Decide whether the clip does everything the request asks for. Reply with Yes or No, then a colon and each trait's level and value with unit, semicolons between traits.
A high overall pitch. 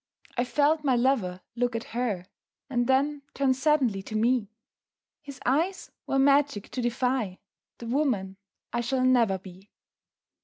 Yes: very high, 250 Hz